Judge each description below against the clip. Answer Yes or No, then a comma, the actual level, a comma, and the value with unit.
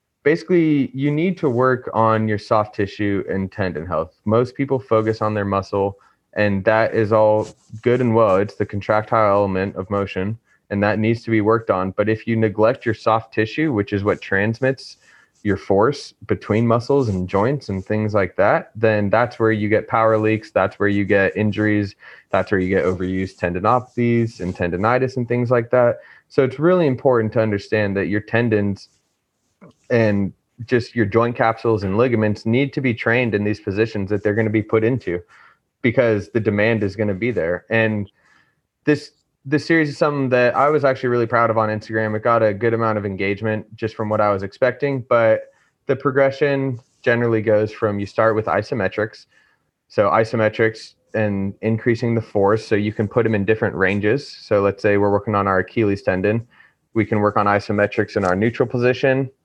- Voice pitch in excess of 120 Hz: No, low, 110 Hz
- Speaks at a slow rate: No, average, 195 wpm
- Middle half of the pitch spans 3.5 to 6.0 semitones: No, average, 2.7 semitones